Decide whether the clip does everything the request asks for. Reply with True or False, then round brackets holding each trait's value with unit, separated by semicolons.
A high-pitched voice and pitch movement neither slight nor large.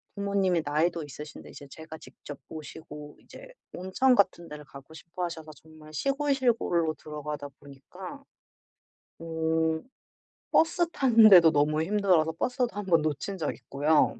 False (160 Hz; 4.7 semitones)